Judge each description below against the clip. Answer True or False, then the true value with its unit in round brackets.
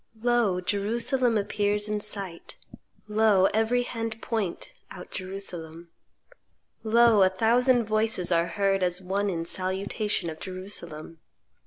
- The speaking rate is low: True (120 wpm)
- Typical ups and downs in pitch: True (3.2 semitones)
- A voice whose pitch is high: True (205 Hz)